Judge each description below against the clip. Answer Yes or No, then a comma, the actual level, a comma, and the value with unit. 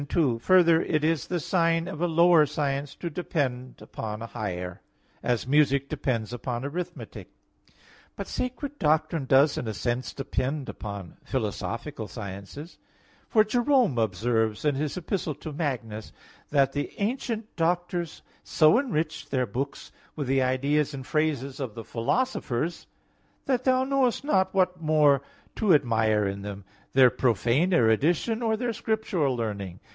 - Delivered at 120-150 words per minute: Yes, average, 145 wpm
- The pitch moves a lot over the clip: Yes, wide, 6.5 semitones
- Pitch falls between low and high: Yes, medium, 145 Hz